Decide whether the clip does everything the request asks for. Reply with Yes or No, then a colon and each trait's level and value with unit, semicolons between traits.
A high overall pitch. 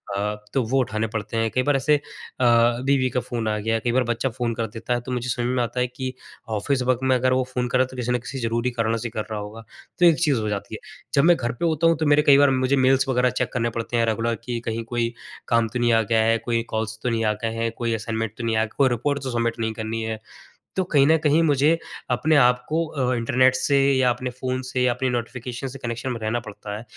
No: low, 120 Hz